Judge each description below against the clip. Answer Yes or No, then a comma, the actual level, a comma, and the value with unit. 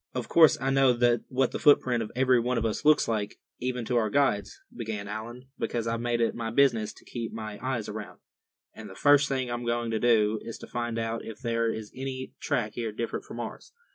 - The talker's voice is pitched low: Yes, low, 120 Hz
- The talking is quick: Yes, fast, 225 wpm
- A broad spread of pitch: No, narrow, 2.4 semitones